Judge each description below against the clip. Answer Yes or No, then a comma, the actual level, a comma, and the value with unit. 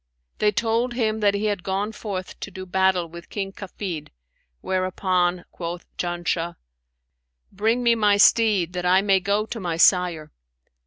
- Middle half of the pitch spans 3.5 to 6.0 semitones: No, average, 2.9 semitones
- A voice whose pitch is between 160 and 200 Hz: Yes, high, 190 Hz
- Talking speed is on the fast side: No, average, 155 wpm